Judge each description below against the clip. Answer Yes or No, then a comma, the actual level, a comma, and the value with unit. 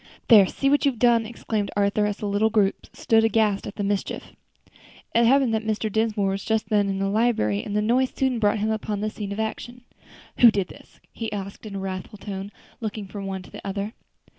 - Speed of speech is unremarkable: No, fast, 220 wpm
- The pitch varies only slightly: Yes, narrow, 2.0 semitones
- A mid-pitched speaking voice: No, high, 210 Hz